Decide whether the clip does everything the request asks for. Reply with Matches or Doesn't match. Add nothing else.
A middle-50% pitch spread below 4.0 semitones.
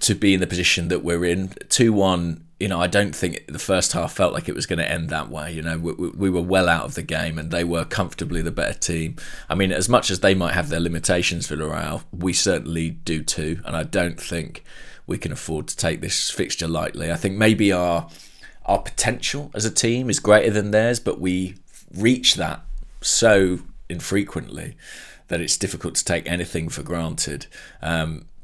Matches